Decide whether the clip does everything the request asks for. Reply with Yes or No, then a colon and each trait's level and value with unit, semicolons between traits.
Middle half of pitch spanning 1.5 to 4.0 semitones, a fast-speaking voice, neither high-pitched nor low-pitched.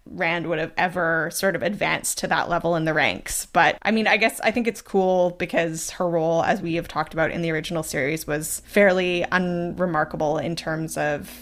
Yes: narrow, 2.4 semitones; fast, 210 wpm; medium, 170 Hz